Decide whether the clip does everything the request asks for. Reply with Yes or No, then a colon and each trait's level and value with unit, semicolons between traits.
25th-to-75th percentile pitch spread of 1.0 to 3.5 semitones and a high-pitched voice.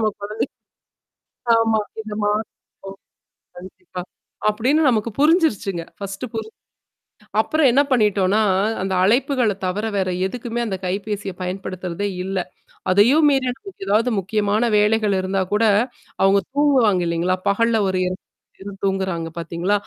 Yes: average, 3.2 semitones; high, 205 Hz